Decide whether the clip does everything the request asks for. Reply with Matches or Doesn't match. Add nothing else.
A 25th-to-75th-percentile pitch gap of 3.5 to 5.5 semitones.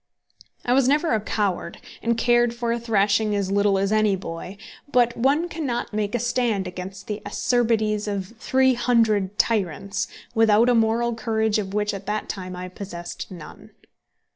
Doesn't match